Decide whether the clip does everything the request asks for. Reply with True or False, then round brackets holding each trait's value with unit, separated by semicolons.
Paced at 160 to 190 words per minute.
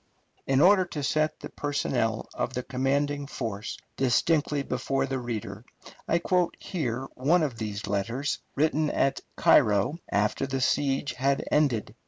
False (145 wpm)